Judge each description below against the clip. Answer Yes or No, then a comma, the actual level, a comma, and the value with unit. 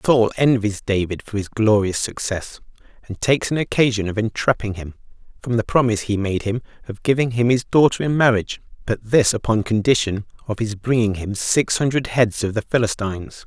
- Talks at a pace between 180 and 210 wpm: Yes, average, 185 wpm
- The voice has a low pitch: Yes, low, 110 Hz